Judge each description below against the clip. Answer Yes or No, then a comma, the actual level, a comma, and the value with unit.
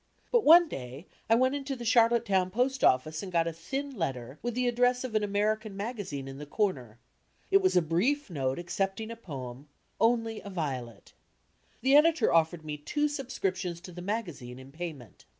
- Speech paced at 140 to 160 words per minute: No, average, 185 wpm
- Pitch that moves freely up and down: Yes, wide, 8.0 semitones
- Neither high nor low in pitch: No, high, 195 Hz